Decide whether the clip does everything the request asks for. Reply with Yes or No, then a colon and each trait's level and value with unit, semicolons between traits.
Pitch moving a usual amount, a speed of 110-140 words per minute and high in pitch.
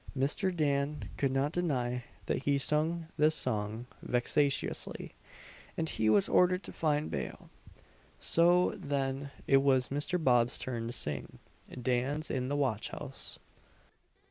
No: average, 3.7 semitones; slow, 135 wpm; medium, 140 Hz